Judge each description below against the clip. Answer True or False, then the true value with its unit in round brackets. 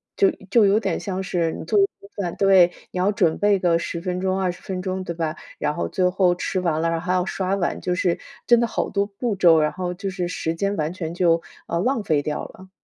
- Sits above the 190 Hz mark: False (185 Hz)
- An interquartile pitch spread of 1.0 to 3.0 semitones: True (2.5 semitones)